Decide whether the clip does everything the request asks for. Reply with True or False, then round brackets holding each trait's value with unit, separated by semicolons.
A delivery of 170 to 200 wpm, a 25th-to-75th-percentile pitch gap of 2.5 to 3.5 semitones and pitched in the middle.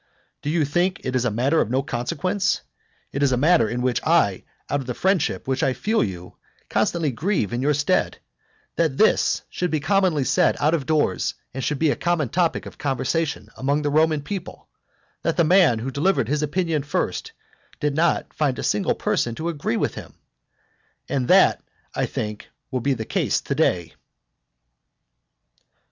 False (180 wpm; 4.6 semitones; 145 Hz)